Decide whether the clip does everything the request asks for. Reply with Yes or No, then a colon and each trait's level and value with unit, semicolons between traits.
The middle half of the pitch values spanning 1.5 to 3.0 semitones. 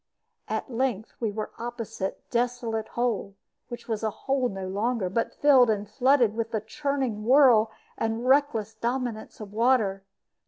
Yes: average, 2.7 semitones